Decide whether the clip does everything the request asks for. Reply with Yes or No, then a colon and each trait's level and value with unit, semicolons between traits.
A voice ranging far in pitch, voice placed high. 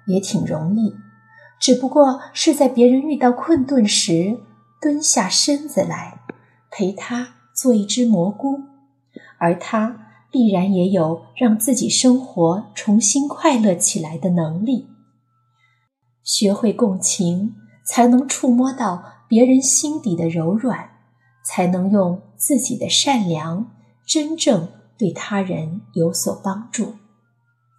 Yes: wide, 6.9 semitones; high, 210 Hz